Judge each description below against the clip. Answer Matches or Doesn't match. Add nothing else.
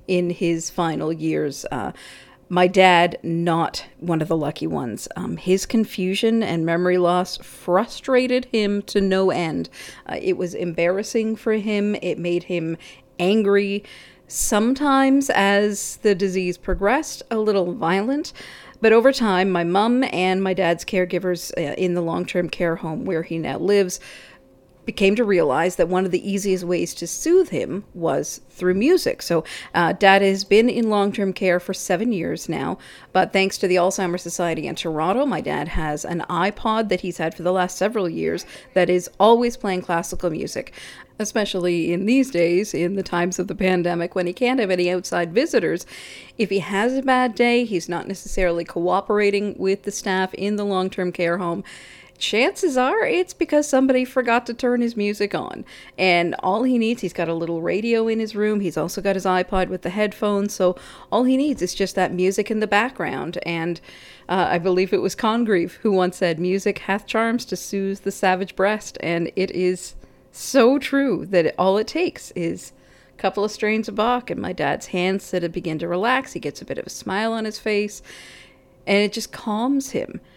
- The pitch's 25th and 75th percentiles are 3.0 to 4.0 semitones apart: Matches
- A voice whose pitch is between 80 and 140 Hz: Doesn't match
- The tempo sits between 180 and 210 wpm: Matches